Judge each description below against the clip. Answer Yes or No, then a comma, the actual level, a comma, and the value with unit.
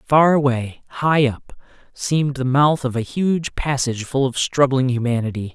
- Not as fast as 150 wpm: No, average, 160 wpm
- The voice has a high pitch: No, low, 135 Hz